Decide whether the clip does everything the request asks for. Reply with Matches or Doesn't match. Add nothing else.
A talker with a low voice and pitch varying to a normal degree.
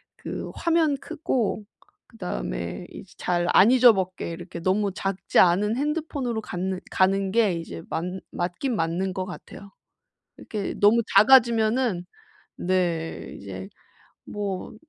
Doesn't match